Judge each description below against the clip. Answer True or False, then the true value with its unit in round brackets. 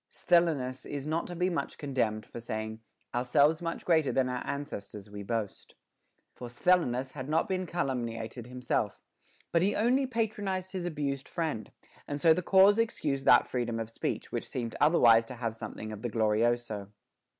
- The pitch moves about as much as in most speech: False (6.7 semitones)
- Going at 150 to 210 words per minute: True (170 wpm)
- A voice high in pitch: False (135 Hz)